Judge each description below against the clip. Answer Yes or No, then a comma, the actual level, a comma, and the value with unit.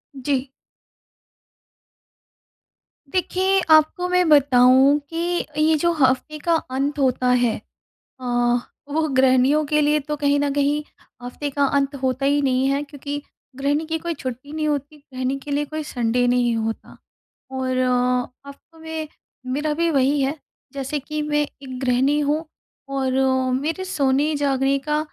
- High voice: Yes, very high, 280 Hz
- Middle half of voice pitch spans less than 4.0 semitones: Yes, average, 2.7 semitones